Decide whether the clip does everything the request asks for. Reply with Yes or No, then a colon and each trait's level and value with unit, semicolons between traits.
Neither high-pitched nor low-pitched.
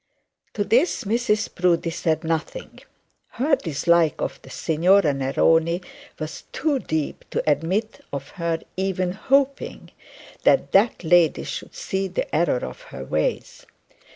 Yes: medium, 175 Hz